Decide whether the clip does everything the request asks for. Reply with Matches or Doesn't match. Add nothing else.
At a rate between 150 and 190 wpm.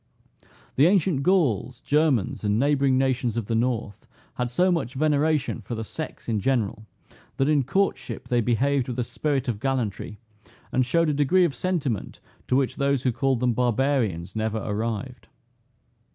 Matches